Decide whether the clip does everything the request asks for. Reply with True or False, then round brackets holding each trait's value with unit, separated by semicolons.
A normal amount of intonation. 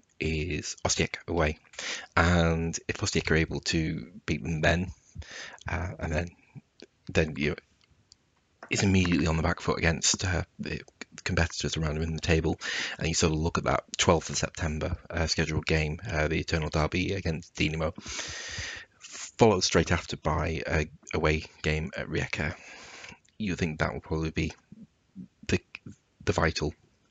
False (1.9 semitones)